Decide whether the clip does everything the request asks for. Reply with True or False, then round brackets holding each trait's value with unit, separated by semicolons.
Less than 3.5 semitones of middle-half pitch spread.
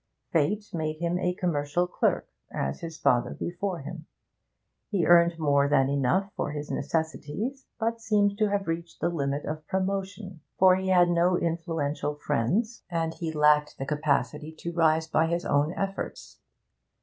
False (3.9 semitones)